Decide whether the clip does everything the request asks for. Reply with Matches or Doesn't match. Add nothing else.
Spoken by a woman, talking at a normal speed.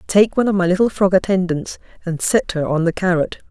Doesn't match